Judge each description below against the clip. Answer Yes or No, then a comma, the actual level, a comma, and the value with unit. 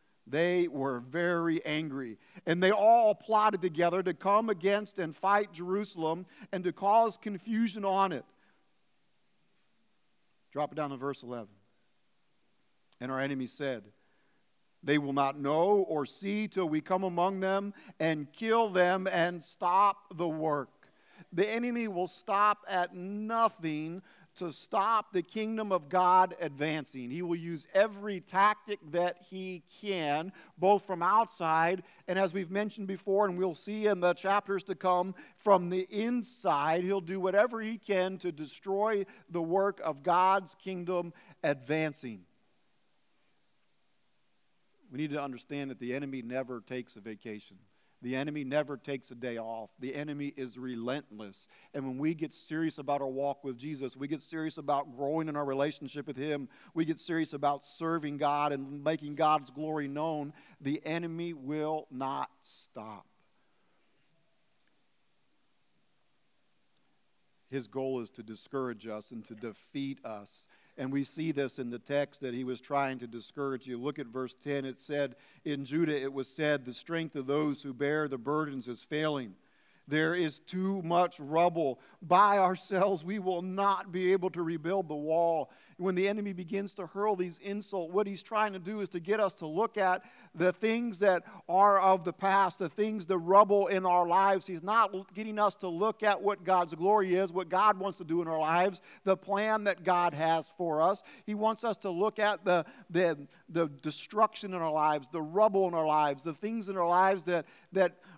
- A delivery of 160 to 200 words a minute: Yes, average, 170 wpm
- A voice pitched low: No, medium, 175 Hz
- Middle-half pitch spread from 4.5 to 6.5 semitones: Yes, average, 5.1 semitones